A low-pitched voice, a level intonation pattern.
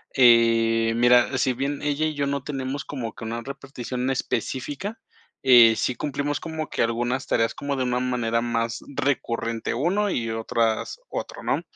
No: low, 125 Hz; average, 3.4 semitones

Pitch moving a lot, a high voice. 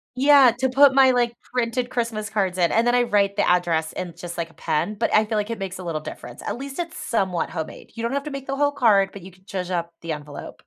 Yes: wide, 5.9 semitones; high, 215 Hz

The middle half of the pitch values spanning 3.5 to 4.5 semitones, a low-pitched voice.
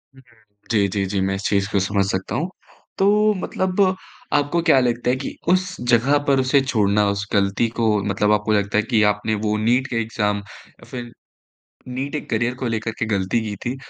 Yes: average, 4.1 semitones; low, 110 Hz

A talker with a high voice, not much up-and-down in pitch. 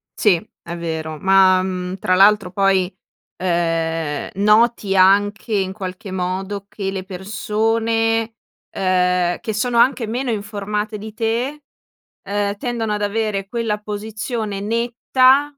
No: high, 205 Hz; average, 3.1 semitones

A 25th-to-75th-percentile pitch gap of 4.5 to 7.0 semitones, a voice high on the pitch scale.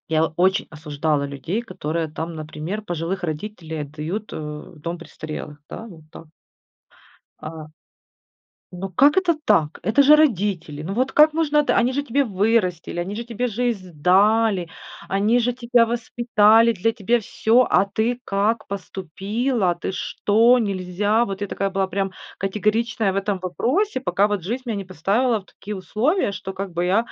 Yes: average, 5.0 semitones; high, 200 Hz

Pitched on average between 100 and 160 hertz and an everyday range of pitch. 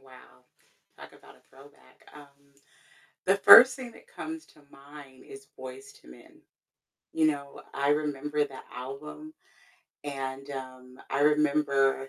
No: medium, 140 Hz; narrow, 2.1 semitones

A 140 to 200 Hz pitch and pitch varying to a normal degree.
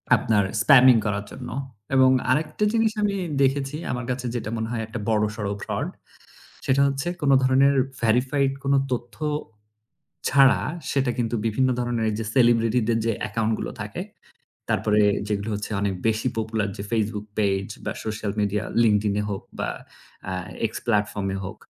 No: low, 115 Hz; average, 3.7 semitones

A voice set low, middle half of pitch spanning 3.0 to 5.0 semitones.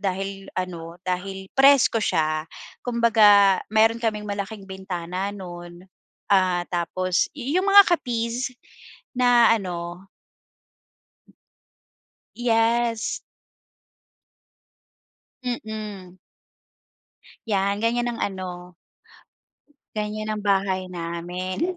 No: high, 200 Hz; average, 3.9 semitones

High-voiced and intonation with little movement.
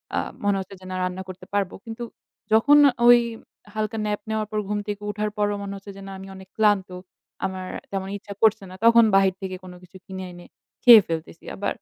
Yes: high, 200 Hz; narrow, 2.2 semitones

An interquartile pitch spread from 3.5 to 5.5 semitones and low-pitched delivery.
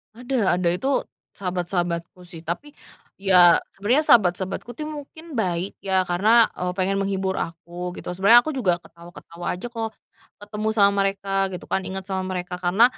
No: average, 3.9 semitones; high, 190 Hz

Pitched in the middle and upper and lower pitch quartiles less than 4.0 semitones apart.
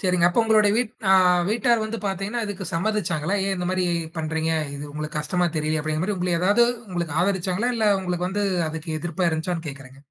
No: medium, 180 Hz; average, 4.3 semitones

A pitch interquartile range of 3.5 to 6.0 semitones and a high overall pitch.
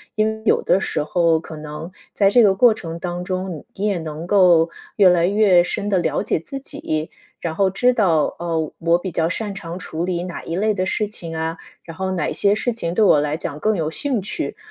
No: average, 3.8 semitones; medium, 180 Hz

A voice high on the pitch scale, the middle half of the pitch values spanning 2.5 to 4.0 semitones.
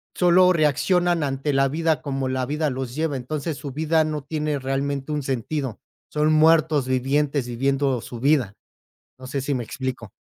No: medium, 140 Hz; average, 2.8 semitones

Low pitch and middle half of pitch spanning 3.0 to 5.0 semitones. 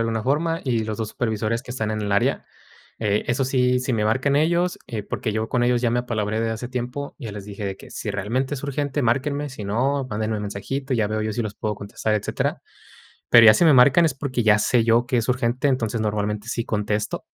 Yes: low, 115 Hz; average, 3.3 semitones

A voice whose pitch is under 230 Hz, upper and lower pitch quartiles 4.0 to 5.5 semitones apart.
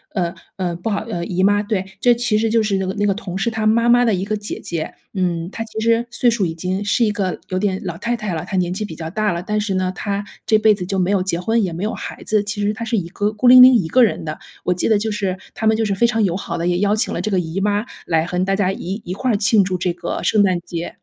No: high, 200 Hz; average, 3.1 semitones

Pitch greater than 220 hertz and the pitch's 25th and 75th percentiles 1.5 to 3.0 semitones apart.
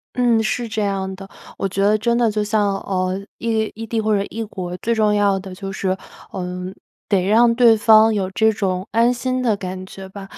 No: high, 210 Hz; average, 2.7 semitones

